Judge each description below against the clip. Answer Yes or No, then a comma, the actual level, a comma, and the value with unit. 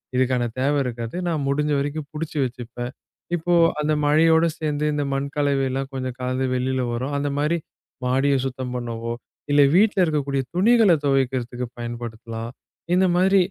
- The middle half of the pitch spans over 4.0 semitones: No, average, 3.3 semitones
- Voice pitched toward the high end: No, low, 135 Hz